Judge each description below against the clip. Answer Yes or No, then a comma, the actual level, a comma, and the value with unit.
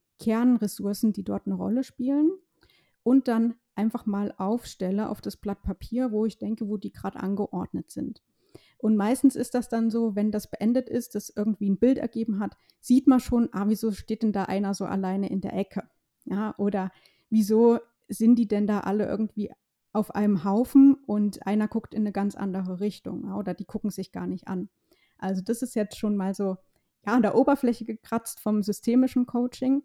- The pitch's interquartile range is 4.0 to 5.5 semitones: No, average, 2.9 semitones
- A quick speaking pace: Yes, fast, 195 wpm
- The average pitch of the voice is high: Yes, high, 215 Hz